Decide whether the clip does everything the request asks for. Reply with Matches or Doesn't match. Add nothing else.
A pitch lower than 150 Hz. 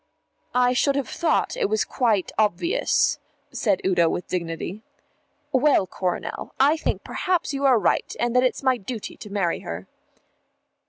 Doesn't match